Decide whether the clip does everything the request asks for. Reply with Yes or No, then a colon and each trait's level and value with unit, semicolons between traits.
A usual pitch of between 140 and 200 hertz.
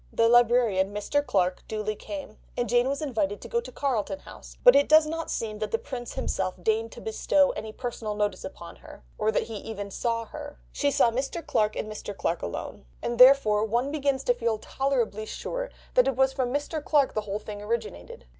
No: high, 230 Hz